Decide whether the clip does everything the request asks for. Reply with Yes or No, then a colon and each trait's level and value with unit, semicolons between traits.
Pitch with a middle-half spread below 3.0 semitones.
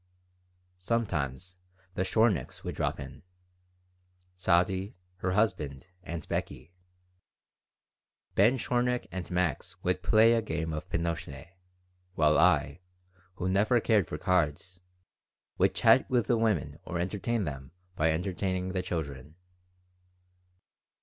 No: average, 4.5 semitones